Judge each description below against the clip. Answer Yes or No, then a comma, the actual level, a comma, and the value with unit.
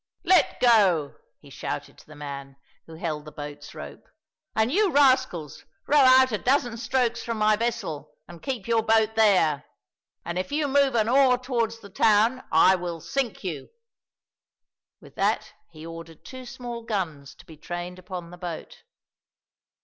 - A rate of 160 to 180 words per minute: Yes, average, 165 wpm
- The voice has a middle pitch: No, high, 215 Hz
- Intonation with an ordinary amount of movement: No, wide, 7.0 semitones